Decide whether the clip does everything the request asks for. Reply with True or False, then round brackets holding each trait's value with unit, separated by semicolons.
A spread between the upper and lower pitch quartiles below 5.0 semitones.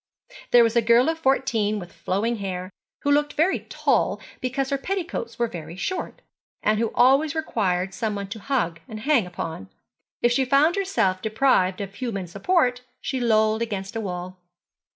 False (5.5 semitones)